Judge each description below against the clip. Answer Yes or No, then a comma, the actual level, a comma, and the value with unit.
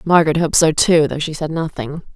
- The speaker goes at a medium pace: No, fast, 225 wpm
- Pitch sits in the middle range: Yes, medium, 155 Hz